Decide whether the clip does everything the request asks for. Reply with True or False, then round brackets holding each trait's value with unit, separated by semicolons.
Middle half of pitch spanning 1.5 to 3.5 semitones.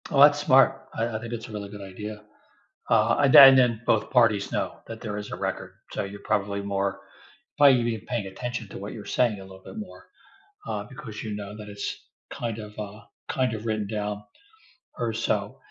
True (2.8 semitones)